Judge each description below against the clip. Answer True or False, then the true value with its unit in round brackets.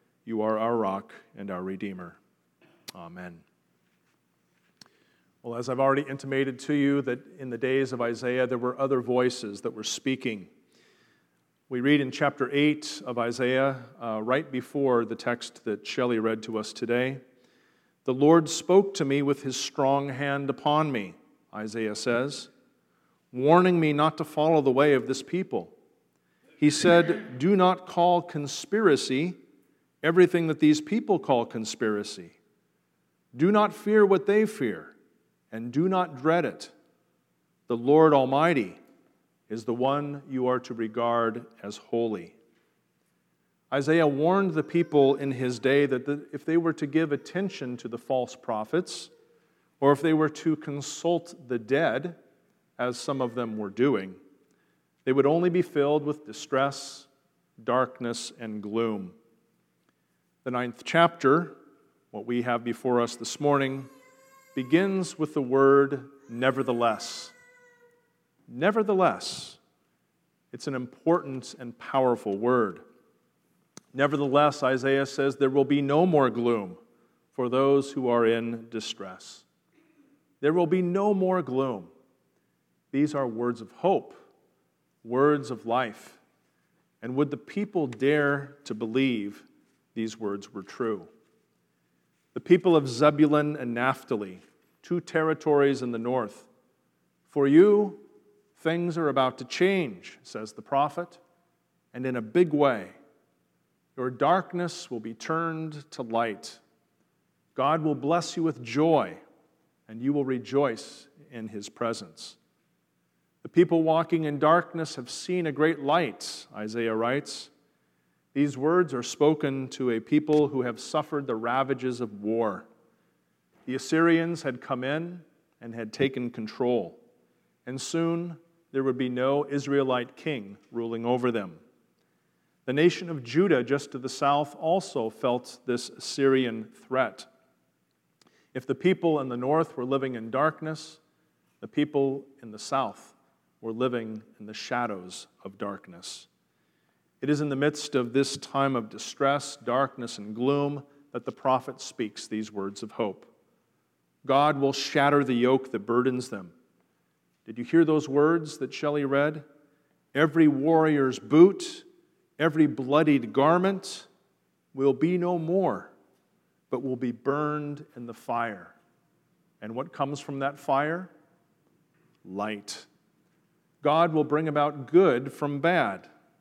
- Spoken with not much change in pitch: False (4.5 semitones)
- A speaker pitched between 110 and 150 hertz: True (140 Hz)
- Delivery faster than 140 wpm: False (135 wpm)